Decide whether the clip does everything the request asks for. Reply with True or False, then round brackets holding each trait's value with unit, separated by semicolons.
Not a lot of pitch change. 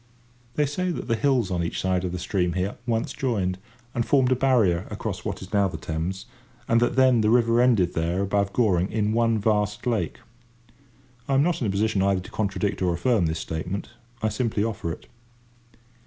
False (4.2 semitones)